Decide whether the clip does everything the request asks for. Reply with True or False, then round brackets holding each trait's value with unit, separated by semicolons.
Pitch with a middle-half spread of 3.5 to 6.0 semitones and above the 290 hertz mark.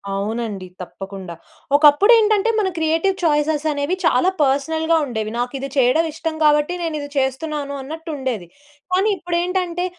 True (4.1 semitones; 300 Hz)